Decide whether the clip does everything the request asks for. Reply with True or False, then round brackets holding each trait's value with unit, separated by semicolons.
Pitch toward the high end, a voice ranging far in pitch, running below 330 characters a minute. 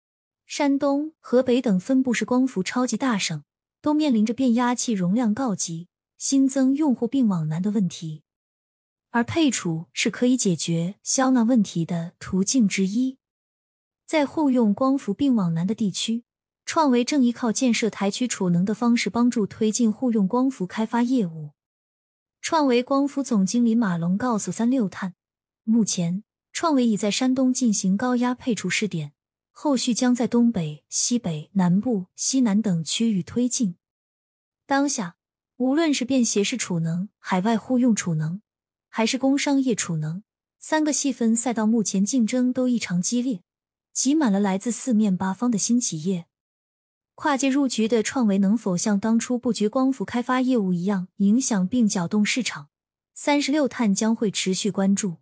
False (230 Hz; 4.9 semitones; 245 characters per minute)